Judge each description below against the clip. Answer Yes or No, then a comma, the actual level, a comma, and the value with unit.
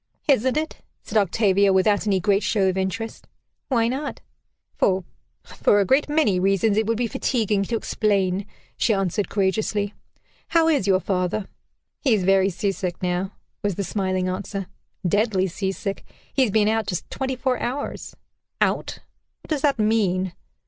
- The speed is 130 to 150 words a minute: No, average, 165 wpm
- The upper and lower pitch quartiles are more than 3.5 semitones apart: No, average, 3.1 semitones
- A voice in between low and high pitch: No, high, 205 Hz